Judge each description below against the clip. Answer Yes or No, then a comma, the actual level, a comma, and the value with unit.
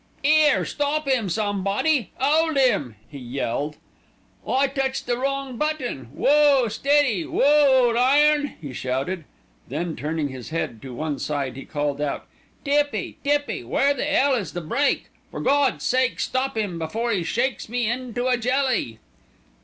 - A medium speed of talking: Yes, average, 155 wpm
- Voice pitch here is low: No, high, 245 Hz